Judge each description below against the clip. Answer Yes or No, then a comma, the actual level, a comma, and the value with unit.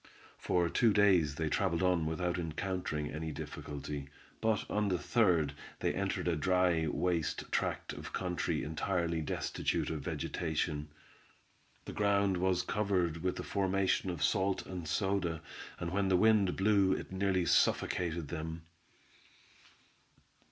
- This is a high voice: No, very low, 90 Hz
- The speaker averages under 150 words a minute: Yes, slow, 135 wpm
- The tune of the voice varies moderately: Yes, average, 3.1 semitones